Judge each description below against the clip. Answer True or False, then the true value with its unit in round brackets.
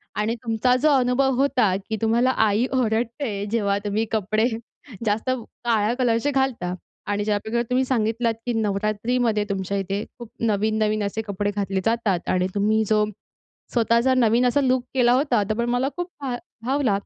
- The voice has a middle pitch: False (225 Hz)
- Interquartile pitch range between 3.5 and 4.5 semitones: False (3.1 semitones)